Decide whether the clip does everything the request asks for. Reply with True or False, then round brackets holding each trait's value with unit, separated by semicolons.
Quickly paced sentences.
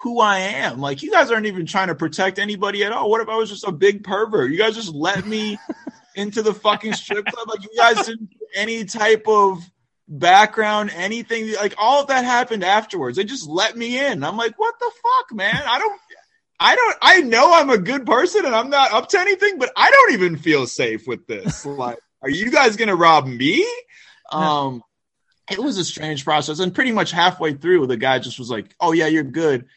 True (225 wpm)